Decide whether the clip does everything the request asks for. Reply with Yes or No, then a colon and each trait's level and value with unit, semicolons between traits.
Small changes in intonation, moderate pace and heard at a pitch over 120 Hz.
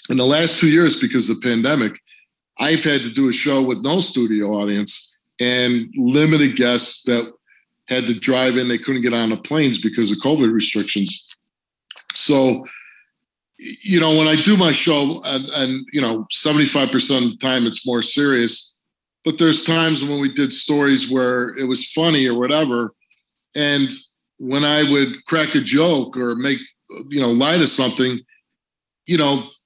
No: average, 3.7 semitones; average, 170 wpm; low, 135 Hz